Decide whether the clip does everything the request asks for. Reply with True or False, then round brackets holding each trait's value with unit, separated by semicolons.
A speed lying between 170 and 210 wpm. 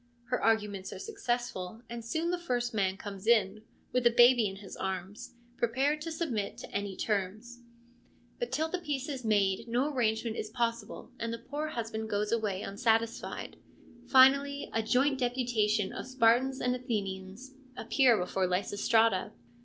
False (155 wpm)